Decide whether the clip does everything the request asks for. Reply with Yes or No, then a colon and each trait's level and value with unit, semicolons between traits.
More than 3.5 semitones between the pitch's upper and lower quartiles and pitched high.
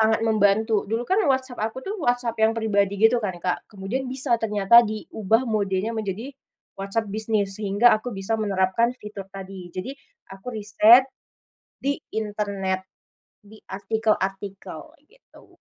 No: average, 3.0 semitones; high, 215 Hz